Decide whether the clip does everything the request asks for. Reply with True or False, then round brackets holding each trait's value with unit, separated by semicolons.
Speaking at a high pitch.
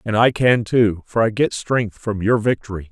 False (110 Hz)